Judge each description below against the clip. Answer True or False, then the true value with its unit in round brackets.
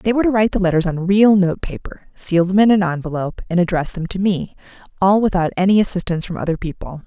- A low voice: False (185 Hz)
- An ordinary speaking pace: False (230 wpm)